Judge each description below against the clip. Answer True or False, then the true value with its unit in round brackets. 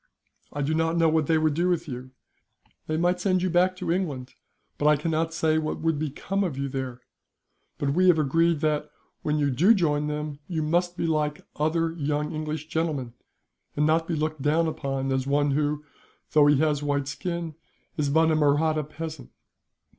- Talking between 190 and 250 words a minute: True (195 wpm)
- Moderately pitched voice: True (155 Hz)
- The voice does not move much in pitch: True (2.0 semitones)